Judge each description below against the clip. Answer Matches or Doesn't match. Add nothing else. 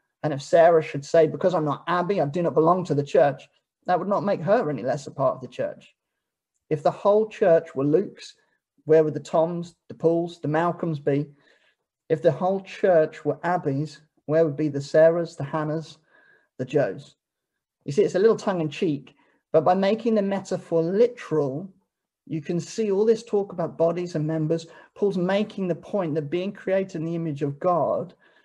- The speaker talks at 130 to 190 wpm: Doesn't match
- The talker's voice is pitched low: Doesn't match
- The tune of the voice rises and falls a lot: Doesn't match